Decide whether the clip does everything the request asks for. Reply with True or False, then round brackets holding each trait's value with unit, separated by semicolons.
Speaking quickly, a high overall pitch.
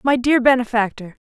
False (140 wpm; 240 Hz)